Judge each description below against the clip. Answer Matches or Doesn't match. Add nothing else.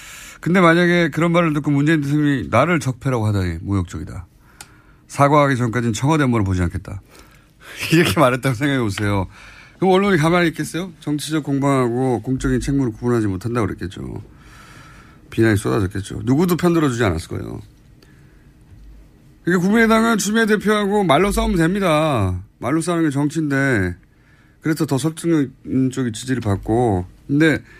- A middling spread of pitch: Doesn't match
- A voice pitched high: Doesn't match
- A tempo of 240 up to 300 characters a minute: Doesn't match